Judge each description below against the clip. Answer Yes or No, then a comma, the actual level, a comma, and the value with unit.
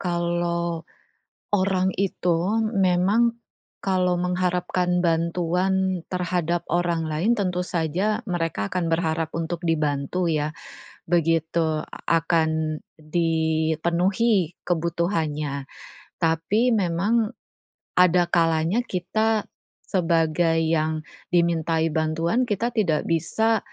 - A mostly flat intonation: Yes, narrow, 2.2 semitones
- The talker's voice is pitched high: No, medium, 170 Hz